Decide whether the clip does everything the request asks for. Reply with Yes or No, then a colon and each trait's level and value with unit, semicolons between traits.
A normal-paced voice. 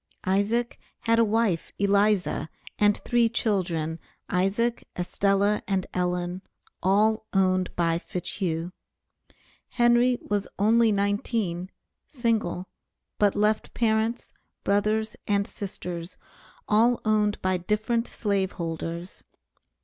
No: slow, 100 wpm